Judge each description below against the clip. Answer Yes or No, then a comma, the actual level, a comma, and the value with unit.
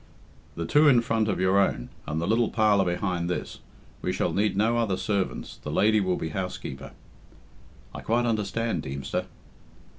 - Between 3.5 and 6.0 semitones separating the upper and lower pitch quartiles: Yes, average, 3.9 semitones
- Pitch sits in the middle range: No, low, 100 Hz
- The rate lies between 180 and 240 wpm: No, average, 170 wpm